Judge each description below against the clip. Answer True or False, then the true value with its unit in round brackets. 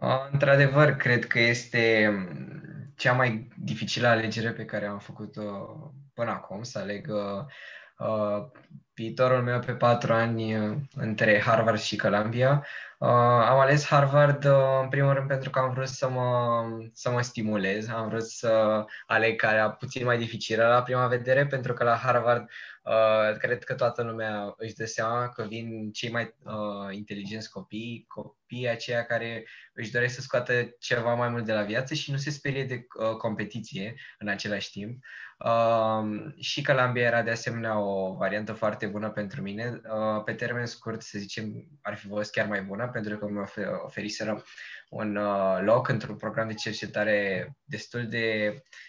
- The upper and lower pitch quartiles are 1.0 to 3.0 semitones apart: True (2.5 semitones)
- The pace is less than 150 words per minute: False (165 wpm)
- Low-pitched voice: True (115 Hz)